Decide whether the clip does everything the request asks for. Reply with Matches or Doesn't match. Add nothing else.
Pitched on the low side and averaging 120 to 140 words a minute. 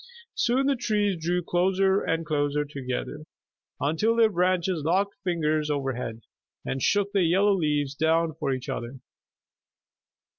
Doesn't match